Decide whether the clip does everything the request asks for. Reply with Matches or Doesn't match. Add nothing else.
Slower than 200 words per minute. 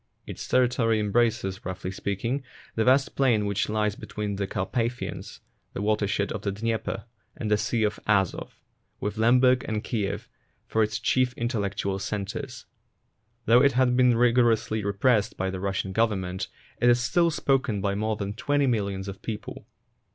Matches